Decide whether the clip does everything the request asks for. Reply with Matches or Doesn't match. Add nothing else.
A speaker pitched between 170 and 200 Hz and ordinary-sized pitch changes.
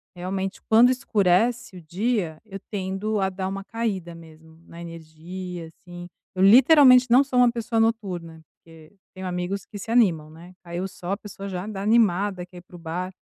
Matches